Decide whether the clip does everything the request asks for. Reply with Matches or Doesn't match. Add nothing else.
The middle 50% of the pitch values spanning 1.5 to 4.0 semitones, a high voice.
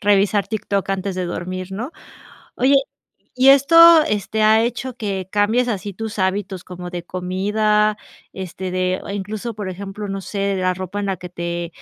Matches